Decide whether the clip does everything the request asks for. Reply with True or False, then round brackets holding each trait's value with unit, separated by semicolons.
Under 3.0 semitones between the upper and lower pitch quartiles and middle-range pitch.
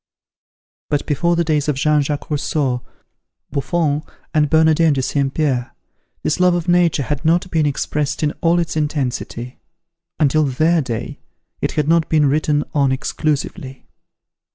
True (2.4 semitones; 150 Hz)